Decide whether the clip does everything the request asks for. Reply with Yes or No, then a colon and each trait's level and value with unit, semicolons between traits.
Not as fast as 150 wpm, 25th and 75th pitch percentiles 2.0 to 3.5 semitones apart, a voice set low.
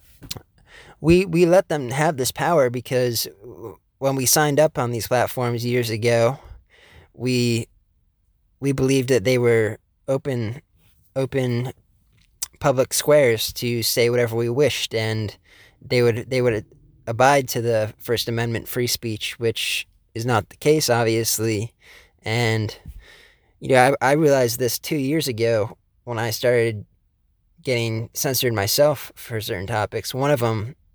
Yes: average, 140 wpm; average, 3.1 semitones; low, 120 Hz